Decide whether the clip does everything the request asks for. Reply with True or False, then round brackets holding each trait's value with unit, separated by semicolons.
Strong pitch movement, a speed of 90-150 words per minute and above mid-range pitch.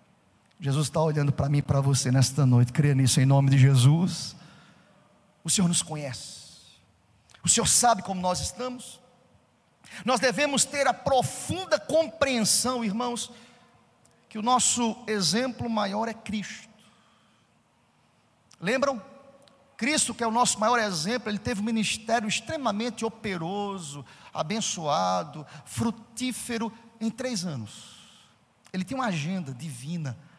True (7.9 semitones; 125 wpm; 205 Hz)